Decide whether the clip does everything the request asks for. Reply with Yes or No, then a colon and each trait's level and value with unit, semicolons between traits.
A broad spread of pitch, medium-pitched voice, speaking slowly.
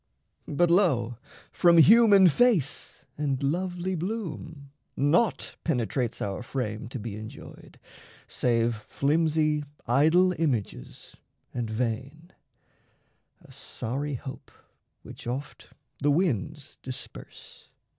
Yes: wide, 5.9 semitones; medium, 145 Hz; slow, 95 wpm